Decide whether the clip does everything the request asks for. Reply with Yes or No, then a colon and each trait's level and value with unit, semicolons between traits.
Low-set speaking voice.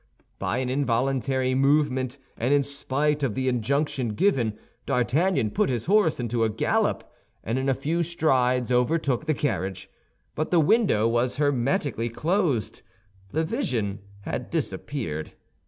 Yes: low, 130 Hz